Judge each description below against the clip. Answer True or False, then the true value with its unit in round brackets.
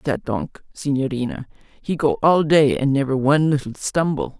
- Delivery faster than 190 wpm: False (165 wpm)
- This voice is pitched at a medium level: True (145 Hz)